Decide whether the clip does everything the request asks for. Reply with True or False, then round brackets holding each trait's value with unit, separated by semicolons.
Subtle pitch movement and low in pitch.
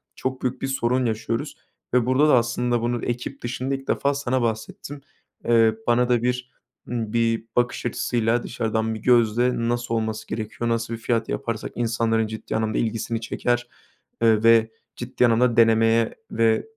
True (1.5 semitones; 115 Hz)